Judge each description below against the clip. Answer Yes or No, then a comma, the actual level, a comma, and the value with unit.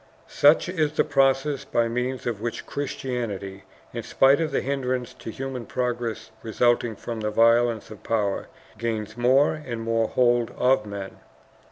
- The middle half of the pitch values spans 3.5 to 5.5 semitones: No, average, 2.9 semitones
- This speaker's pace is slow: No, average, 155 wpm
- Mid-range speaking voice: No, low, 120 Hz